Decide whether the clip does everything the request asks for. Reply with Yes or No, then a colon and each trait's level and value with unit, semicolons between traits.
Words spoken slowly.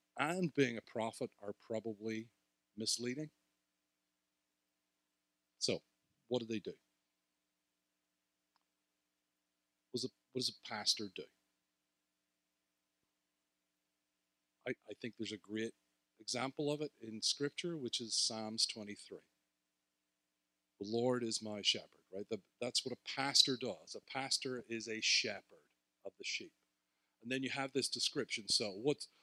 Yes: slow, 130 wpm